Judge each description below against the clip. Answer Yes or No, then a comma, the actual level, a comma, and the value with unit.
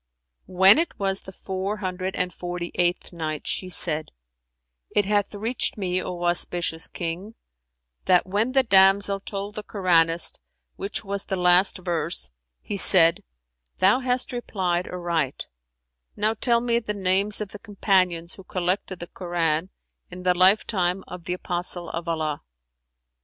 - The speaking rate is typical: Yes, average, 145 wpm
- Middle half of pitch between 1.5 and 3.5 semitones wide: Yes, narrow, 2.5 semitones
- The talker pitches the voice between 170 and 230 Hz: Yes, medium, 185 Hz